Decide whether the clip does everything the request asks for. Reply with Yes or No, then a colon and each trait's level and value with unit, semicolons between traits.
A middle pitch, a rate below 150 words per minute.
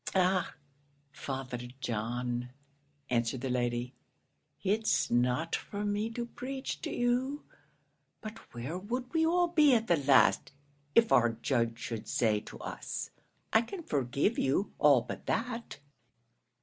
Yes: medium, 155 Hz; slow, 135 wpm